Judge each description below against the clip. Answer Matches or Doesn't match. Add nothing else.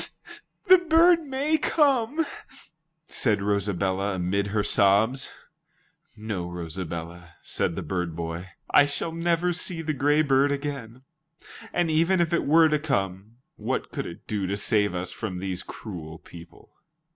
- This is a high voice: Doesn't match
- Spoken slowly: Doesn't match